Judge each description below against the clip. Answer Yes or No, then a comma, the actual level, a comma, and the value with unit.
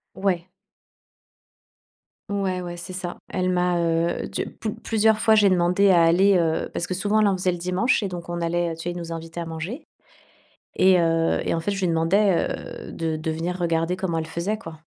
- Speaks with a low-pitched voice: No, medium, 175 Hz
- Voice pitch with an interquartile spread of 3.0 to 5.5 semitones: No, narrow, 2.4 semitones